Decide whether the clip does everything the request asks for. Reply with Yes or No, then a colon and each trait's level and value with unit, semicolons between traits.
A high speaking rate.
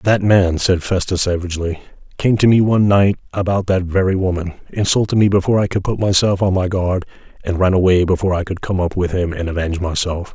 Yes: fast, 215 wpm